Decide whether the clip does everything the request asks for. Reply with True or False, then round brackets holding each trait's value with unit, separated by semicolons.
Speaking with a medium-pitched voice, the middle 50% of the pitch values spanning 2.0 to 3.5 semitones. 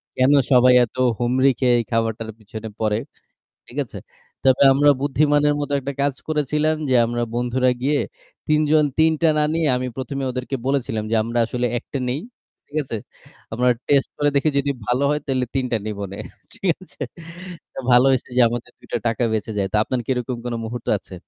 False (130 Hz; 3.2 semitones)